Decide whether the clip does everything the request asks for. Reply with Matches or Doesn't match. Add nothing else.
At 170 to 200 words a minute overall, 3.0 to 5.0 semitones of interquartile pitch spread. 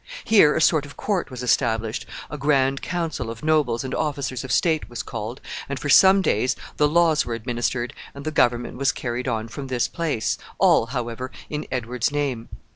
Matches